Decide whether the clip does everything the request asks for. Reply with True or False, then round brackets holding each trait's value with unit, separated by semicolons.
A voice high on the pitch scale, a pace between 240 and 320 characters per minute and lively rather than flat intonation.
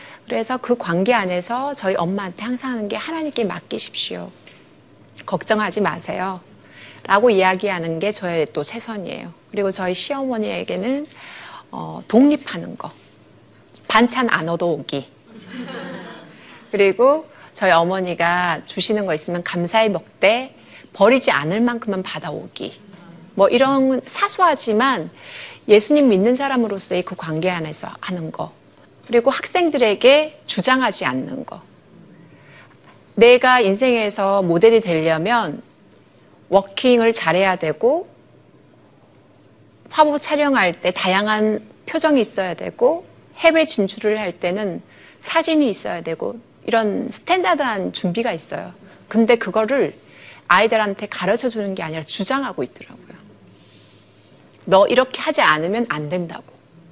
True (215 Hz; 275 characters per minute; 6.0 semitones)